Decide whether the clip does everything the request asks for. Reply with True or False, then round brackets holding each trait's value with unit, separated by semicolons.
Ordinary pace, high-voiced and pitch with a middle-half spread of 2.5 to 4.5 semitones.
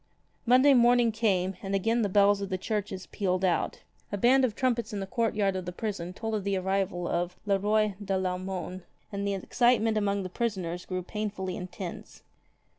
True (190 wpm; 200 Hz; 2.9 semitones)